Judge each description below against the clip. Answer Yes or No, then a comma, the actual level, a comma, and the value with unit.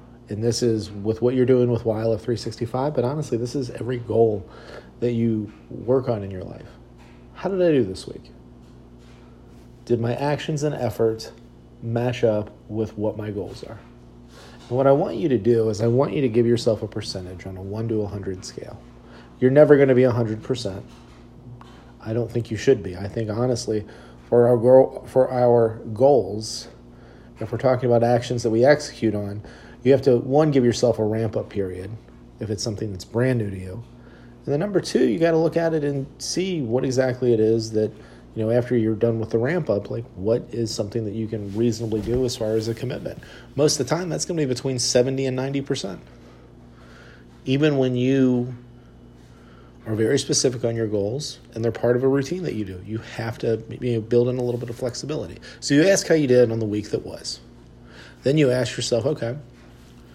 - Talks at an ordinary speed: No, fast, 210 wpm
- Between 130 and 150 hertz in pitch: No, low, 115 Hz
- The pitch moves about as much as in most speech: Yes, average, 3.6 semitones